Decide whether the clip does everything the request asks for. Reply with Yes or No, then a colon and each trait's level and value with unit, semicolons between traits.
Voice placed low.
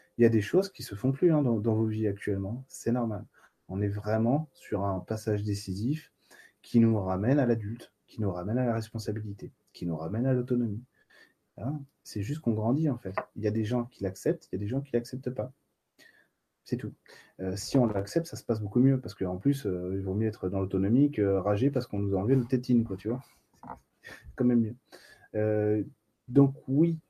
Yes: low, 115 Hz